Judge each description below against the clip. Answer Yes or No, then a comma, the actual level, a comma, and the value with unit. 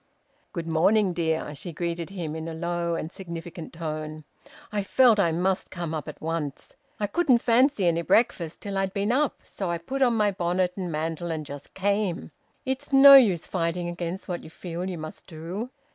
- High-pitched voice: No, medium, 175 Hz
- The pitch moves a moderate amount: Yes, average, 3.6 semitones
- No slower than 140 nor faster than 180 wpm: No, average, 190 wpm